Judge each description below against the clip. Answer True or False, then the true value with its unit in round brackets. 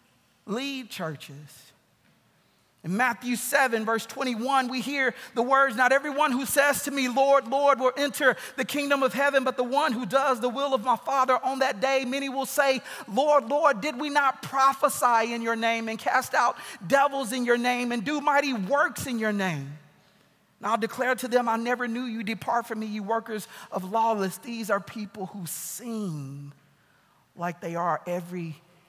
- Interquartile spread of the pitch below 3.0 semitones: False (3.8 semitones)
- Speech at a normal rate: True (185 wpm)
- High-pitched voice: True (250 Hz)